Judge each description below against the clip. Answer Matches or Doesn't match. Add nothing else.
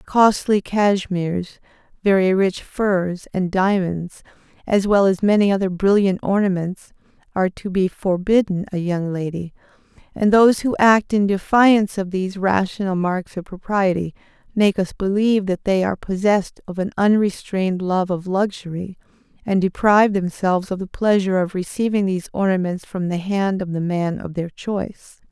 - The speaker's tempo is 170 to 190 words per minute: Doesn't match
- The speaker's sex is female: Matches